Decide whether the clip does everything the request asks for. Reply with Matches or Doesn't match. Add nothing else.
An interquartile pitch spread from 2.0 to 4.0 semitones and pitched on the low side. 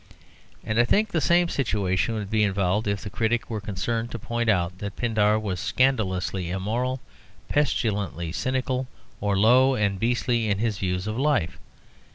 Matches